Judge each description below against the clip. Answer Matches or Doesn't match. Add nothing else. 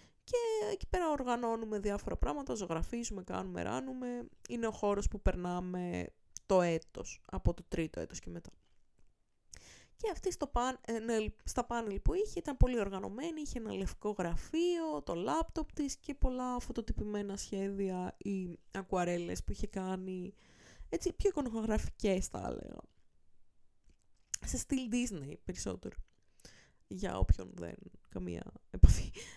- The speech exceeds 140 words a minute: Doesn't match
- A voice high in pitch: Matches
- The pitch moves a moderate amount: Doesn't match